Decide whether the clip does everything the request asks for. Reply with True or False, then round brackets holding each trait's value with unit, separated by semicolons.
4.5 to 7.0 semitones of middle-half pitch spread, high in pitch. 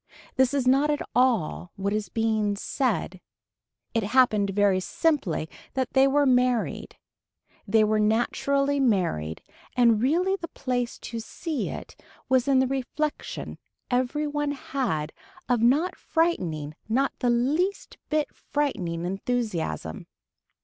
True (5.0 semitones; 245 Hz)